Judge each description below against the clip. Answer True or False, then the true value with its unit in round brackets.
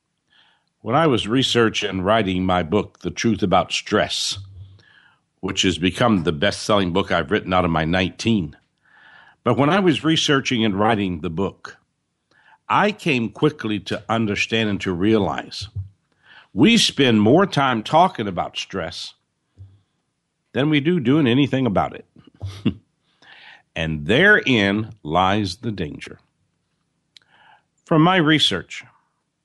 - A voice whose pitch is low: True (110 Hz)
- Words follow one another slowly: True (130 wpm)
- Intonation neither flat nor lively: False (6.5 semitones)